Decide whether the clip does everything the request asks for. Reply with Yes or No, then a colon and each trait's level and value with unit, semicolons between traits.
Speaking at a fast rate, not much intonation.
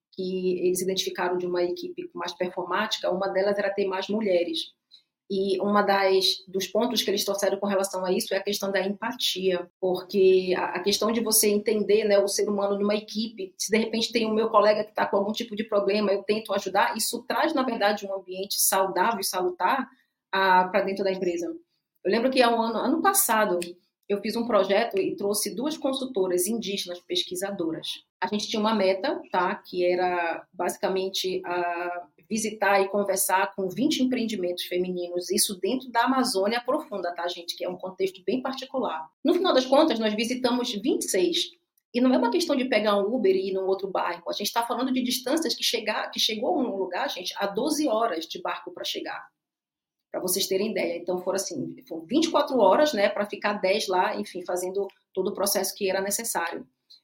No: fast, 200 wpm; average, 3.5 semitones